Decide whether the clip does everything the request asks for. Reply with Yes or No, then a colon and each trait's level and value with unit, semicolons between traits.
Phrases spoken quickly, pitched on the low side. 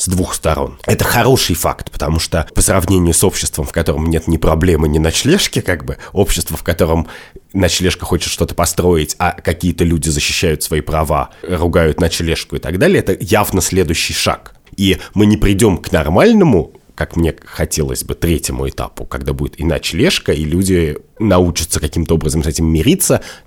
Yes: fast, 170 wpm; very low, 85 Hz